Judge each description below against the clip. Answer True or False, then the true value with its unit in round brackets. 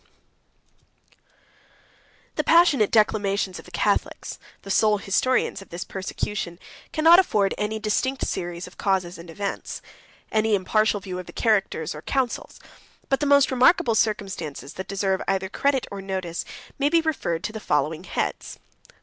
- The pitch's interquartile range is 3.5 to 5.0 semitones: True (4.2 semitones)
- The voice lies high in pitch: True (200 Hz)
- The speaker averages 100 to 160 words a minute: True (155 wpm)